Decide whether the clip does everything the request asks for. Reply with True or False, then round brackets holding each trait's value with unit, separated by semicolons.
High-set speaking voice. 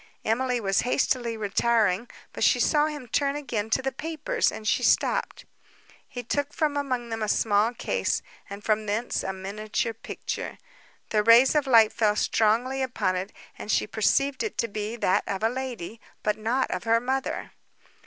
True (230 Hz)